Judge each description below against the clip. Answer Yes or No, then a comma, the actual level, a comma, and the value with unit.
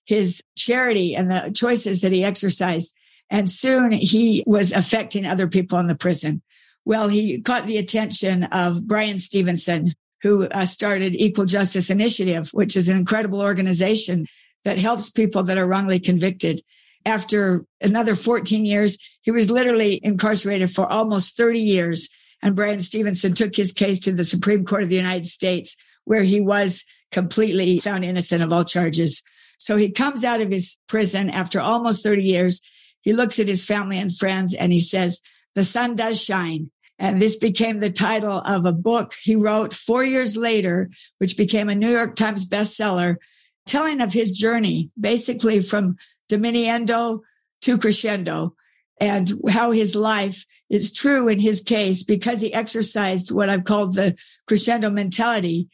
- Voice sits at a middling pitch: No, high, 205 Hz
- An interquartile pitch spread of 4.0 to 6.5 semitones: No, average, 2.8 semitones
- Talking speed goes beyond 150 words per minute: Yes, average, 160 wpm